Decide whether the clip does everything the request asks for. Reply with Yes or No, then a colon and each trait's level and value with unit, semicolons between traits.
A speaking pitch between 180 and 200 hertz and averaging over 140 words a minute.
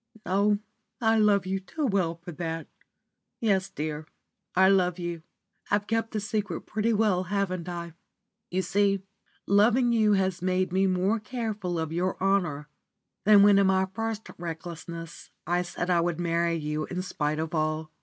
Yes: medium, 185 Hz; average, 165 wpm